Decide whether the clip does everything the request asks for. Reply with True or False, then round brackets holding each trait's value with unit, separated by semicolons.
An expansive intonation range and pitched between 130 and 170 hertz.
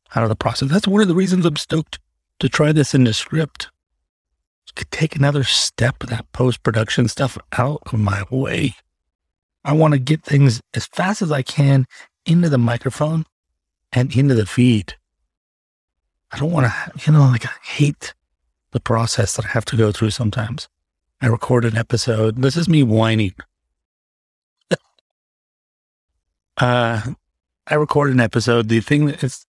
False (8.5 semitones; 120 Hz)